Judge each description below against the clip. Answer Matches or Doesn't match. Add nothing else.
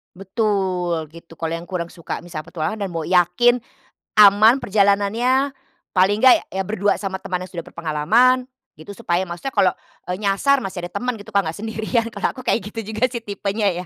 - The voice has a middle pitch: Doesn't match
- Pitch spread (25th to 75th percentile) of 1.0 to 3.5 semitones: Doesn't match